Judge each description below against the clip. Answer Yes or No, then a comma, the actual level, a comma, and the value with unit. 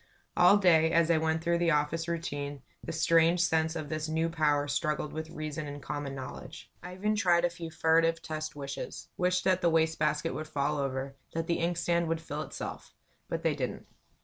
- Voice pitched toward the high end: No, medium, 160 Hz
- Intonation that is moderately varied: No, narrow, 2.0 semitones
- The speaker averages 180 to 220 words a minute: Yes, average, 200 wpm